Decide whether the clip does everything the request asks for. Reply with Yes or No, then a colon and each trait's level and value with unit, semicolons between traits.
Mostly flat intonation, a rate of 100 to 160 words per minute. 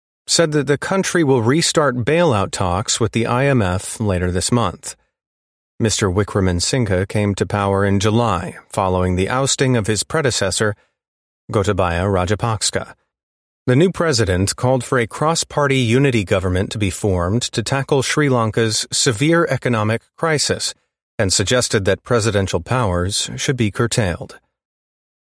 No: average, 5.0 semitones; slow, 135 wpm